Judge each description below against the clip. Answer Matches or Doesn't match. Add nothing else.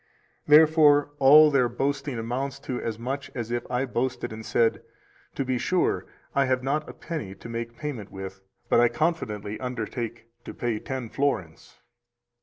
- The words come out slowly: Doesn't match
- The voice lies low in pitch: Matches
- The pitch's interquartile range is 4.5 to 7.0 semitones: Doesn't match